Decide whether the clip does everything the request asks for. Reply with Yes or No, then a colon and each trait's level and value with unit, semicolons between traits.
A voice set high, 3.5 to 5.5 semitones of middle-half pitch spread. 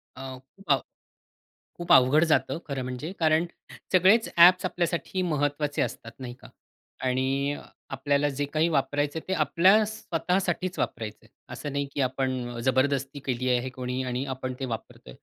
No: medium, 140 Hz; average, 4.2 semitones